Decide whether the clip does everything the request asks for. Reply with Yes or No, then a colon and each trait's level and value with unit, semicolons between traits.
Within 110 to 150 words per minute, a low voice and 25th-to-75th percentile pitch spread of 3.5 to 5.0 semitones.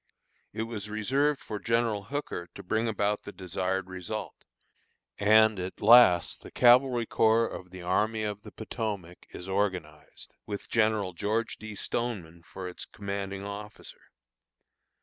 No: average, 140 wpm; low, 105 Hz; average, 3.0 semitones